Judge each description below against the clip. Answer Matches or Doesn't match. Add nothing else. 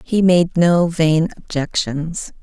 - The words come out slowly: Matches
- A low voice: Doesn't match